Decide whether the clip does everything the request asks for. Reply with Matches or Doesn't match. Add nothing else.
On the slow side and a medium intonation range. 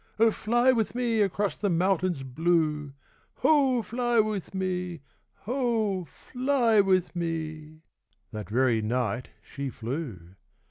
Doesn't match